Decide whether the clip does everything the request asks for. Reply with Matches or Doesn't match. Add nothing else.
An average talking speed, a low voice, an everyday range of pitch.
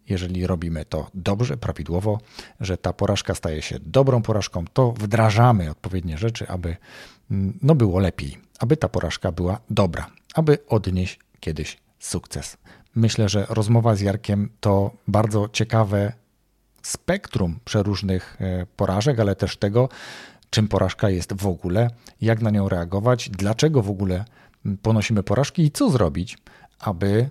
Matches